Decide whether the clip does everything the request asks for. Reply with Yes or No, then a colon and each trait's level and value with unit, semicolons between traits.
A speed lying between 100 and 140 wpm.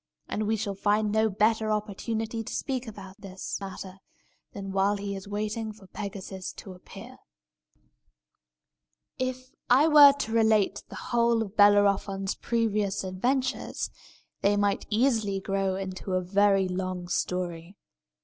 Yes: slow, 135 wpm